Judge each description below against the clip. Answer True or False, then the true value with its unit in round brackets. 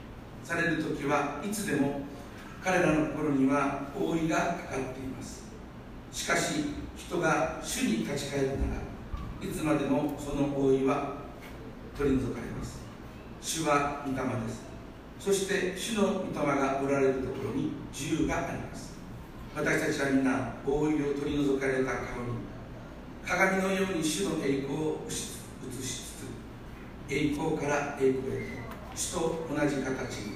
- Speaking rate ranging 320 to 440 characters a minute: False (255 characters per minute)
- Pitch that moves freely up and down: False (2.5 semitones)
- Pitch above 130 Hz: True (140 Hz)